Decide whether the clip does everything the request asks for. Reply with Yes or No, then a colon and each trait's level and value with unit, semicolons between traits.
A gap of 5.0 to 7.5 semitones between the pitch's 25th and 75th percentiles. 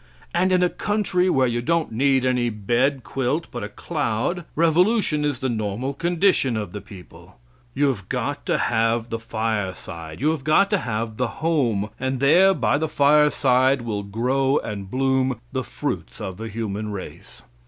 Yes: wide, 5.5 semitones